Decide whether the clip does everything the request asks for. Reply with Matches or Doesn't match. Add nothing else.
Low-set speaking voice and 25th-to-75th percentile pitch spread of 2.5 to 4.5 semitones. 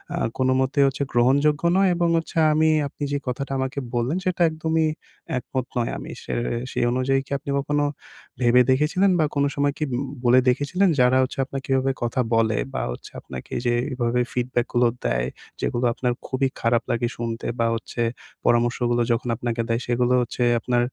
Matches